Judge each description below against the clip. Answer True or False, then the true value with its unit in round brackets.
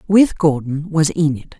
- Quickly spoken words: False (150 wpm)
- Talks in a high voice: False (155 Hz)